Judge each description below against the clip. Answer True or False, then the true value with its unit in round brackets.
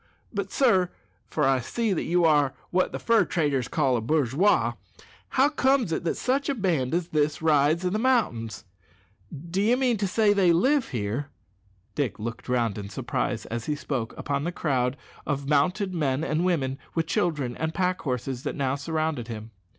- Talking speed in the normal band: True (180 wpm)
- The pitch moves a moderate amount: False (5.9 semitones)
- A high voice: False (155 Hz)